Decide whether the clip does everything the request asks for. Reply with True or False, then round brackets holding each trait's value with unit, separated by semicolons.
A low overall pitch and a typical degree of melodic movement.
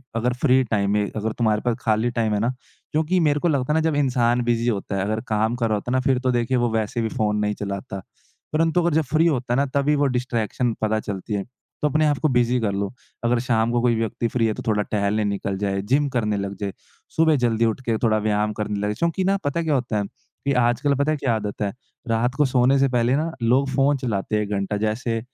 True (120 Hz; 4.0 semitones)